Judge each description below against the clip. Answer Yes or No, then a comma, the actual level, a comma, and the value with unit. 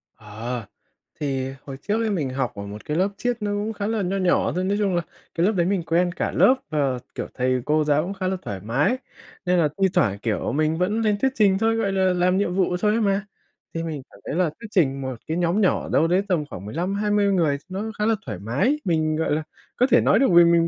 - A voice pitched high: No, medium, 175 Hz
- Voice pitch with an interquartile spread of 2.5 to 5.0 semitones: No, wide, 5.6 semitones